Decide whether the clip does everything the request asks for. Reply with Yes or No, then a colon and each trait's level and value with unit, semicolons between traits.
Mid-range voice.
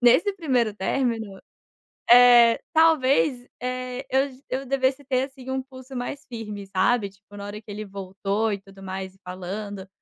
No: high, 235 Hz